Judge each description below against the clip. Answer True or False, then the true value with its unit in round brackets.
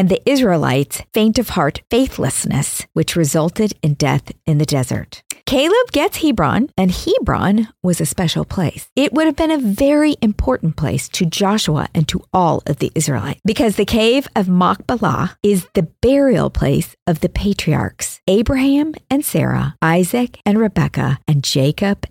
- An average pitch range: False (7.5 semitones)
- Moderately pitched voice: False (195 Hz)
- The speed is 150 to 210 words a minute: True (160 wpm)